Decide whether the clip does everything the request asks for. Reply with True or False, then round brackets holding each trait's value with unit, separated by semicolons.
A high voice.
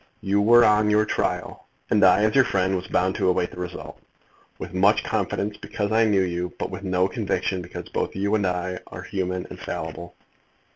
False (95 Hz)